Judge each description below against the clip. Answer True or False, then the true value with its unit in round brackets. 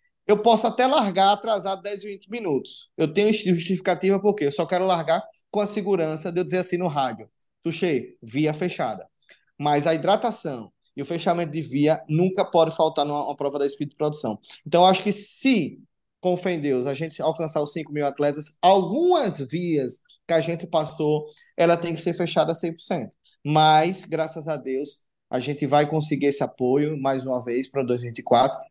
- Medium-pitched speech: True (165 Hz)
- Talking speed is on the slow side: False (185 wpm)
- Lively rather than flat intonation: False (4.3 semitones)